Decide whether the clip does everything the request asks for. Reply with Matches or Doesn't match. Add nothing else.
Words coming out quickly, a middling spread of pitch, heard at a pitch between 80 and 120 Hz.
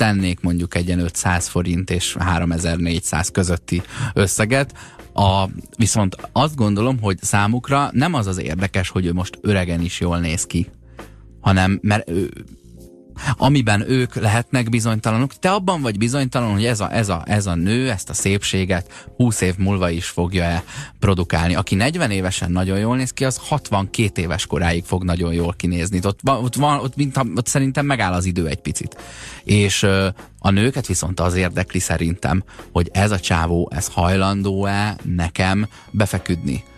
Matches